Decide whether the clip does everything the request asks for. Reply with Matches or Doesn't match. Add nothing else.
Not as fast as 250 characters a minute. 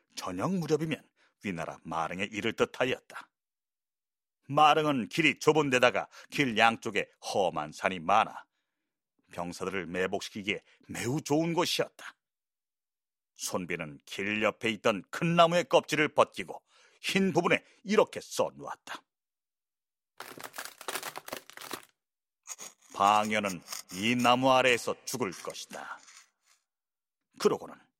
Matches